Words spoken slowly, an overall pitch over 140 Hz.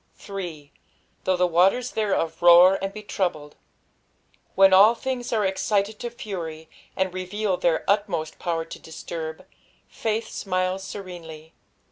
Yes: slow, 130 wpm; medium, 185 Hz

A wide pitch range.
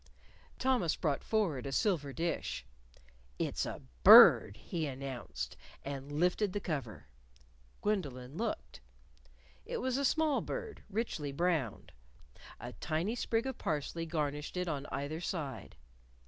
Yes: wide, 6.7 semitones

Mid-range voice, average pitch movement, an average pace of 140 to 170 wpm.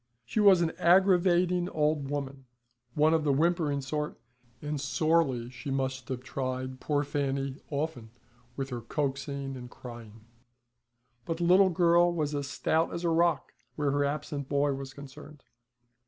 Yes: medium, 145 Hz; average, 3.5 semitones; average, 155 wpm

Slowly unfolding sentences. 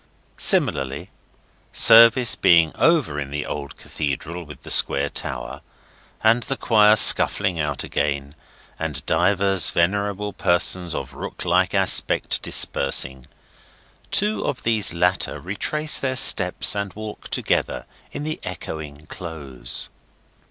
Yes: slow, 120 wpm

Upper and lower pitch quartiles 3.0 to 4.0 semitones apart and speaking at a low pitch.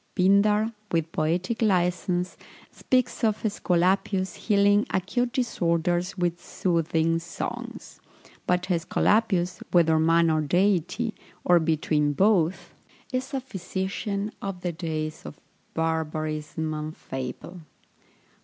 No: average, 3.6 semitones; medium, 180 Hz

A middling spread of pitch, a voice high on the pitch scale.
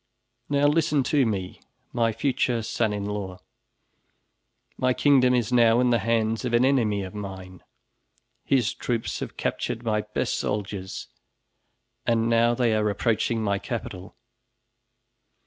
No: average, 3.1 semitones; low, 115 Hz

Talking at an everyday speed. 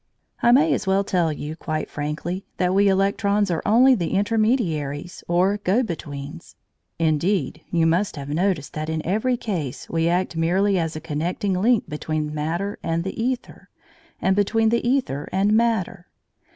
Yes: average, 165 wpm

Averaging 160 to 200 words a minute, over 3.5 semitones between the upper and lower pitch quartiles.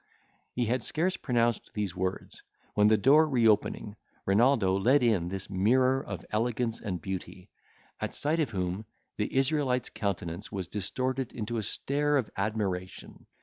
No: average, 150 wpm; average, 5.0 semitones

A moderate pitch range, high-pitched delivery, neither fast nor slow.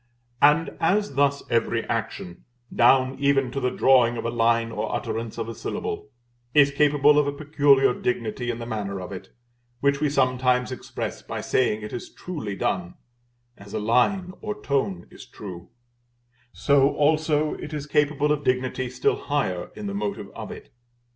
No: average, 4.1 semitones; low, 130 Hz; average, 170 wpm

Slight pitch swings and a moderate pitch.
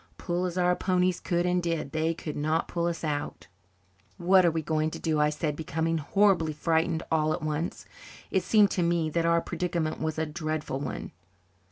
Yes: narrow, 2.0 semitones; medium, 165 Hz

